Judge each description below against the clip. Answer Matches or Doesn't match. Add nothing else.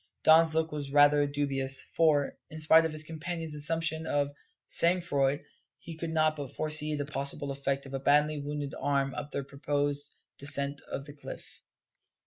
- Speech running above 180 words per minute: Doesn't match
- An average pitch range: Doesn't match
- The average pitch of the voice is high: Doesn't match